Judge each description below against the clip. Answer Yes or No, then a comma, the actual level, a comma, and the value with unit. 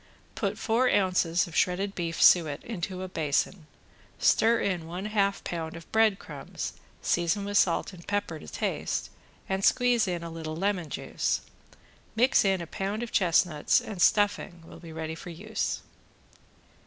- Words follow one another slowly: No, average, 160 wpm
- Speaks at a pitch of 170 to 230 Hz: Yes, medium, 185 Hz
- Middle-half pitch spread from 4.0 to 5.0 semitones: No, average, 3.5 semitones